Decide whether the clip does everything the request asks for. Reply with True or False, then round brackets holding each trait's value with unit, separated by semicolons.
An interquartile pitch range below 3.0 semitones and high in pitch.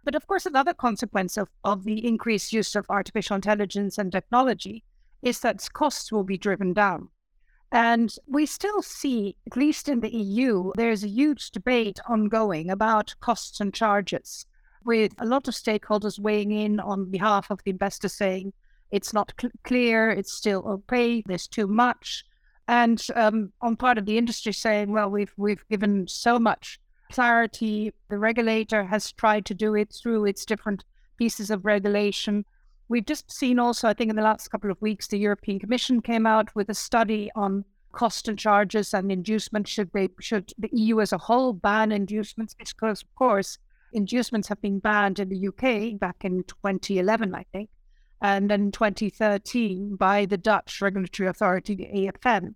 True (2.4 semitones; 215 Hz)